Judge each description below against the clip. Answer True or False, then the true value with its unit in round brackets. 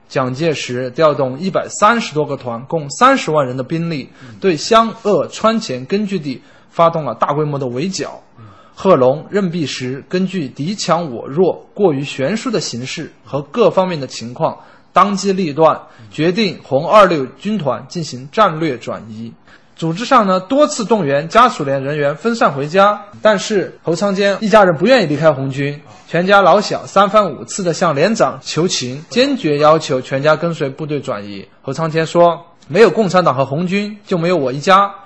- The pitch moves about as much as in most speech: False (6.4 semitones)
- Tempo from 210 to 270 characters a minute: True (265 characters per minute)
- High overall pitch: False (165 Hz)